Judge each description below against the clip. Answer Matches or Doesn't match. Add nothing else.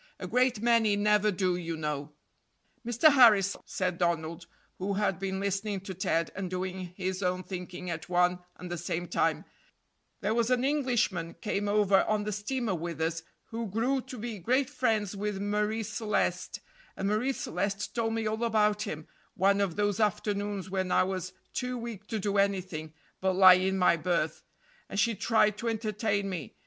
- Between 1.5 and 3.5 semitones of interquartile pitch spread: Matches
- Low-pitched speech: Doesn't match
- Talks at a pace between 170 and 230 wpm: Matches